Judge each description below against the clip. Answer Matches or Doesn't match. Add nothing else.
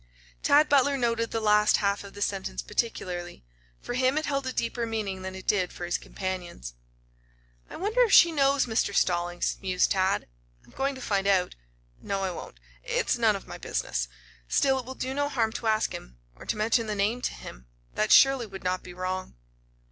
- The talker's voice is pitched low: Doesn't match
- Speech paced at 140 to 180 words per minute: Doesn't match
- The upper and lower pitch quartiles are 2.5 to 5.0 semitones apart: Doesn't match